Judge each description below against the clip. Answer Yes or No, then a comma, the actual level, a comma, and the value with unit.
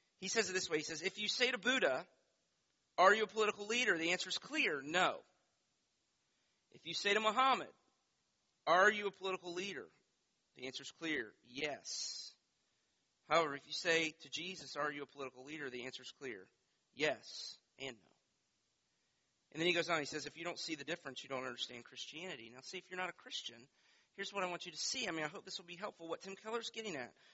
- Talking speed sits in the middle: No, fast, 215 wpm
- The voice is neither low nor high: Yes, medium, 175 Hz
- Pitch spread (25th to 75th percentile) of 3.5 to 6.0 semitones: Yes, average, 4.8 semitones